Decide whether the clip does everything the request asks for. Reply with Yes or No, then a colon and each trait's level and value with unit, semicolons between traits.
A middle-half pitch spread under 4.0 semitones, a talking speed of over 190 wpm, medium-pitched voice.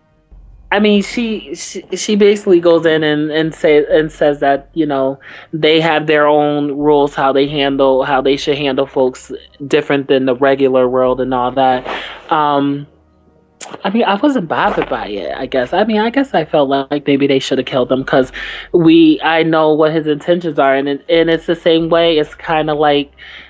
Yes: average, 3.4 semitones; average, 200 wpm; medium, 150 Hz